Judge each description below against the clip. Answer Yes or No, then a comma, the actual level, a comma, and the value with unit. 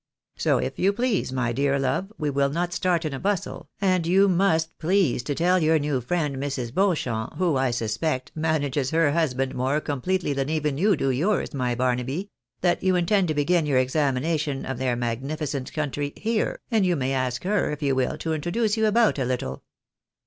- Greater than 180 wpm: Yes, average, 200 wpm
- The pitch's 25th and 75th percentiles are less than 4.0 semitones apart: No, average, 5.1 semitones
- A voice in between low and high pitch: Yes, medium, 150 Hz